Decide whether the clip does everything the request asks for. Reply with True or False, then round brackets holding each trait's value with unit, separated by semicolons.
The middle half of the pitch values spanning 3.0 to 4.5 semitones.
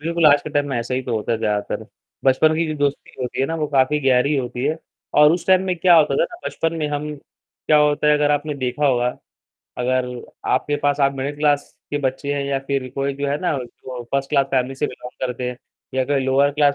False (2.4 semitones)